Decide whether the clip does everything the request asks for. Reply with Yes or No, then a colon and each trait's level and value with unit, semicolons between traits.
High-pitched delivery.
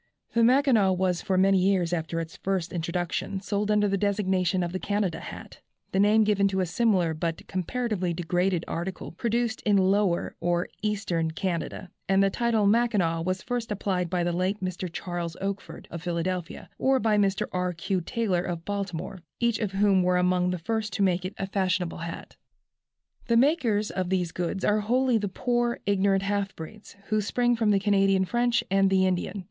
Yes: high, 195 Hz